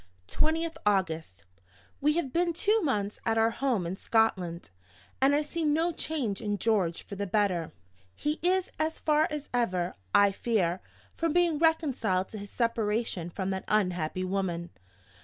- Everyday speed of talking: Yes, average, 160 wpm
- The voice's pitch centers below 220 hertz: No, high, 225 Hz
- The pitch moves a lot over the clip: Yes, wide, 8.4 semitones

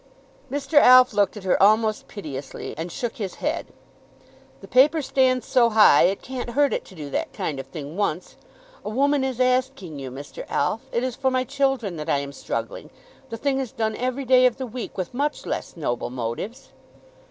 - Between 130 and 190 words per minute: No, average, 200 wpm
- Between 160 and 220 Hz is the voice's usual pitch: No, high, 235 Hz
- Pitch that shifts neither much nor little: No, wide, 7.2 semitones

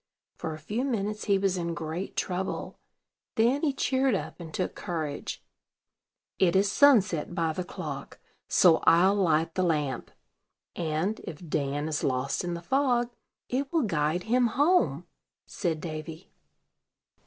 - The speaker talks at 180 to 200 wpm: No, average, 145 wpm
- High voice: No, medium, 180 Hz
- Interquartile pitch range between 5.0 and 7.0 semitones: Yes, wide, 5.6 semitones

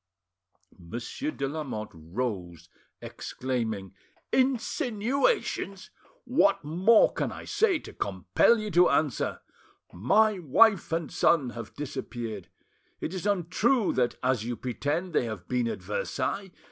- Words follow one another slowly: Yes, slow, 120 wpm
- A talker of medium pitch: Yes, medium, 150 Hz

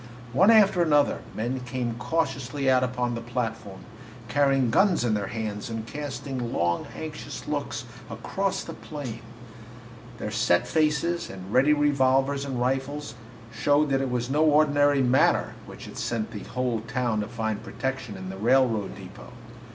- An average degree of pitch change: Yes, average, 4.2 semitones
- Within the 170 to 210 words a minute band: No, average, 155 wpm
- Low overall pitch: Yes, low, 125 Hz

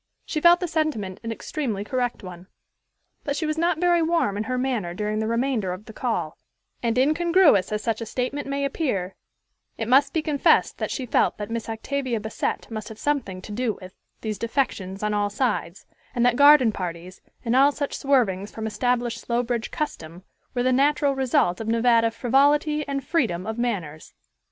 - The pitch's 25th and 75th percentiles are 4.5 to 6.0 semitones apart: Yes, average, 4.9 semitones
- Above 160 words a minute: Yes, average, 185 wpm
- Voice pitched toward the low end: No, high, 235 Hz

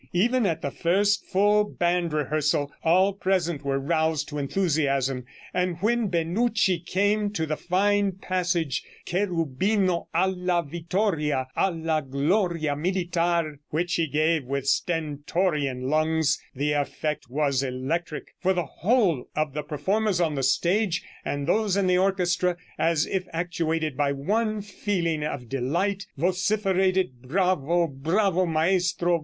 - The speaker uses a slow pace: Yes, slow, 130 wpm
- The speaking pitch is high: No, medium, 170 Hz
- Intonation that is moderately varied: Yes, average, 4.0 semitones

